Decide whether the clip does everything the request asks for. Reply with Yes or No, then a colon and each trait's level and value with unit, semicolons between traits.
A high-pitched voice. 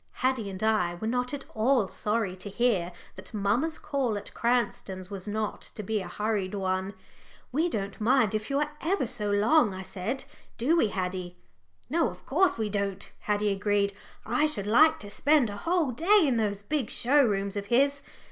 Yes: high, 215 Hz